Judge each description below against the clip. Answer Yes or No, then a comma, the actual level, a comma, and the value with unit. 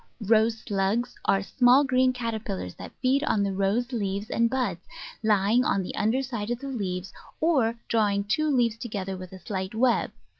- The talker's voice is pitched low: No, high, 220 Hz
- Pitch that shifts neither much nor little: Yes, average, 3.9 semitones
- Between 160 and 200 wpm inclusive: Yes, average, 180 wpm